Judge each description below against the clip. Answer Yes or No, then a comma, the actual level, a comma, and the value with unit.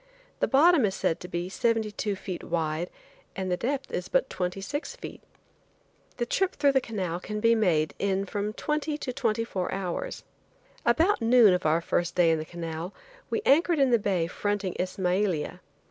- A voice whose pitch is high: Yes, high, 200 Hz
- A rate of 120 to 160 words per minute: No, average, 185 wpm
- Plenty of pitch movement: Yes, wide, 5.9 semitones